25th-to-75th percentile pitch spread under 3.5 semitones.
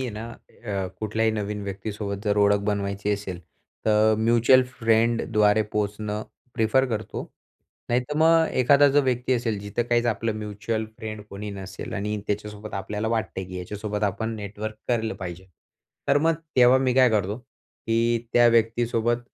Yes: narrow, 2.5 semitones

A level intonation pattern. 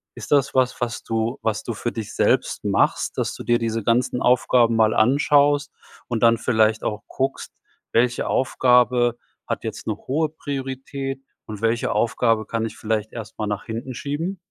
No: average, 3.0 semitones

